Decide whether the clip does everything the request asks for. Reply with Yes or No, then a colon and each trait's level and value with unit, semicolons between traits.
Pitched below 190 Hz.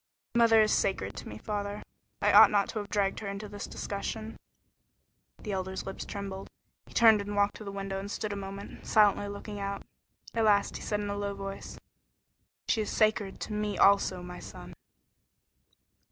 No: high, 200 Hz